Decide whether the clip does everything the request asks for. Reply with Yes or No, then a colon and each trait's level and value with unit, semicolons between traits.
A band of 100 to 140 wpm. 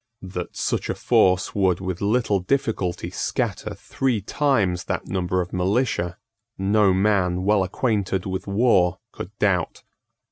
Yes: slow, 135 wpm